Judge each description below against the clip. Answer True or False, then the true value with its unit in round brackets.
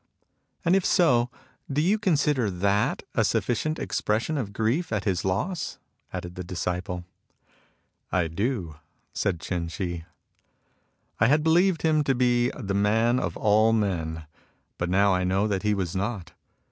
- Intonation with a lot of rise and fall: True (6.4 semitones)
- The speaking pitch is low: True (105 Hz)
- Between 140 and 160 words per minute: True (155 wpm)